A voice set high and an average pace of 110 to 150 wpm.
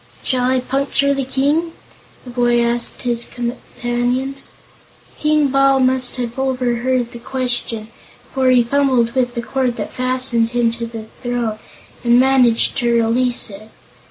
Yes: very high, 250 Hz; average, 145 wpm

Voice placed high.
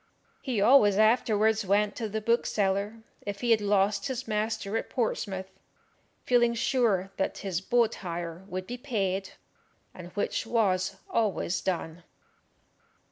Yes: high, 210 Hz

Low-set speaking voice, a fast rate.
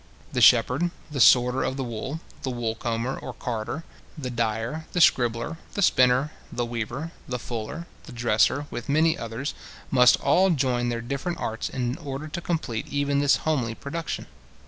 No: low, 125 Hz; average, 170 wpm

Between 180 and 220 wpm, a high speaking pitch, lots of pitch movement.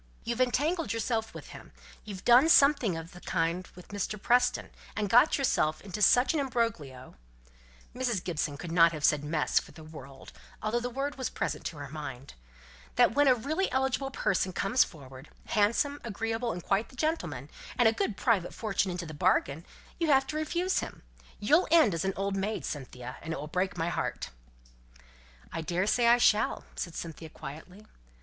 Yes: average, 185 wpm; high, 205 Hz; wide, 7.3 semitones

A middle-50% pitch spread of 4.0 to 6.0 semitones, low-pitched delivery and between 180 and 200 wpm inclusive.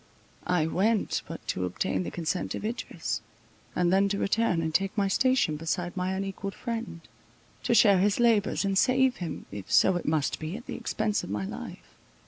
No: average, 4.7 semitones; high, 190 Hz; average, 190 wpm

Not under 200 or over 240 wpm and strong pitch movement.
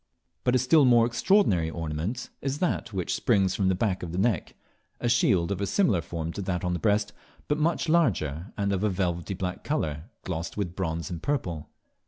Yes: fast, 205 wpm; wide, 5.8 semitones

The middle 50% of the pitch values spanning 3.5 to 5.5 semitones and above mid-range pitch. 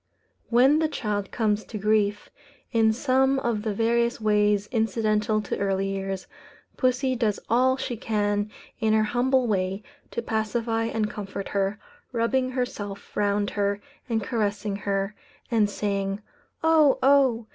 No: average, 2.7 semitones; high, 215 Hz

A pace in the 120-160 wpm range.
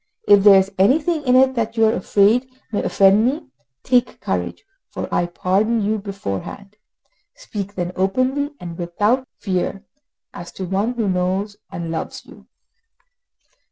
Yes: average, 150 wpm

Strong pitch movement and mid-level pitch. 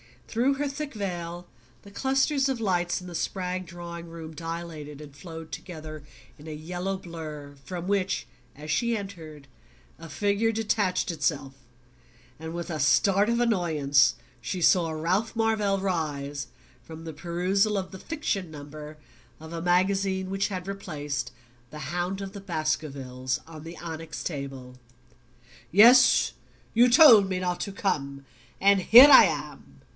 No: average, 4.3 semitones; medium, 175 Hz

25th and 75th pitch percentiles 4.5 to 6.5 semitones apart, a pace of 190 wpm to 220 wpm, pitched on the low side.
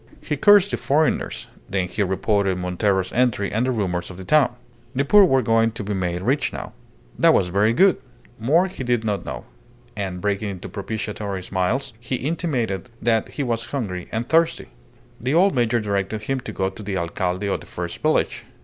Yes: average, 5.2 semitones; average, 195 wpm; low, 110 Hz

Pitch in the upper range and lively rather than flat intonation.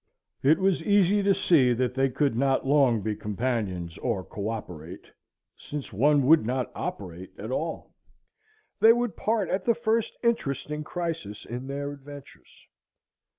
No: low, 135 Hz; wide, 7.0 semitones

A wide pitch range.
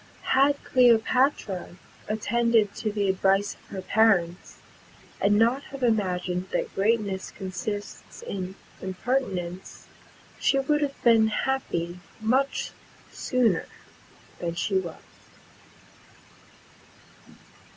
No: average, 4.4 semitones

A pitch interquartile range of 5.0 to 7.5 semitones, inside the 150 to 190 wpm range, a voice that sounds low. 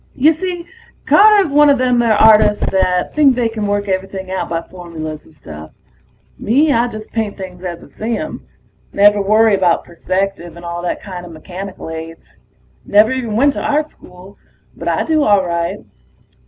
No: average, 5.3 semitones; average, 175 wpm; high, 205 Hz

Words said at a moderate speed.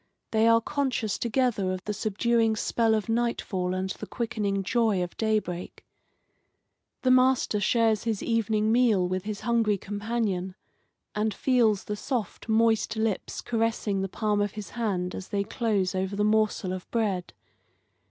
Yes: average, 150 wpm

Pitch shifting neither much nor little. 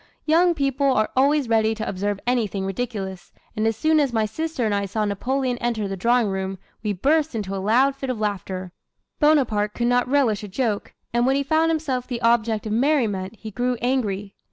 Yes: average, 4.5 semitones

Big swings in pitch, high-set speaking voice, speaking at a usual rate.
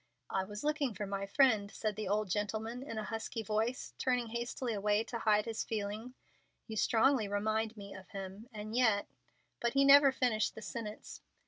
No: narrow, 2.5 semitones; high, 220 Hz; average, 190 wpm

